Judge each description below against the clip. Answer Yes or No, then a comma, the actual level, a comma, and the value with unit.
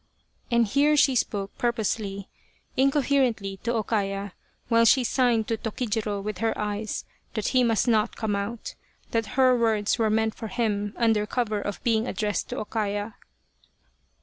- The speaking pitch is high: Yes, high, 220 Hz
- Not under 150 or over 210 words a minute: Yes, average, 160 wpm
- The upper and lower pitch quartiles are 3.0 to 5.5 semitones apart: No, narrow, 2.4 semitones